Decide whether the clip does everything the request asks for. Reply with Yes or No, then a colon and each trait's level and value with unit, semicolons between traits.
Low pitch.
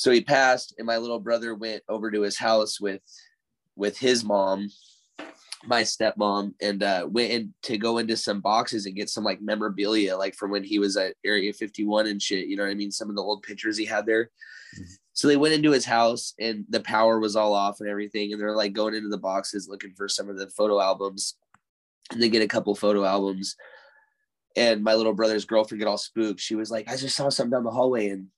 Yes: low, 110 Hz